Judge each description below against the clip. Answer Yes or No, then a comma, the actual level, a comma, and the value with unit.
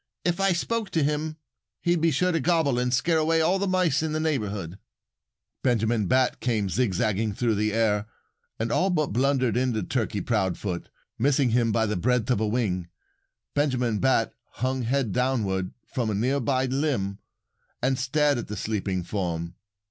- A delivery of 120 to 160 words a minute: No, average, 170 wpm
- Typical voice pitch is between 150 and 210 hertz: No, low, 125 Hz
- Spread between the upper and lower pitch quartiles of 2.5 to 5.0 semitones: No, wide, 5.6 semitones